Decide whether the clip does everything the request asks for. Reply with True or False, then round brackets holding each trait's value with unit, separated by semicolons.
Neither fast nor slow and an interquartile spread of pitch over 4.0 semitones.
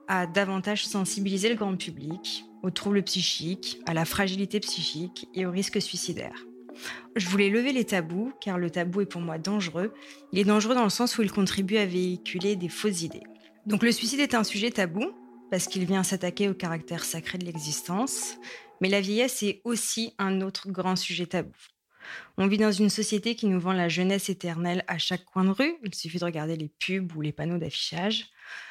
False (200 wpm; 3.1 semitones)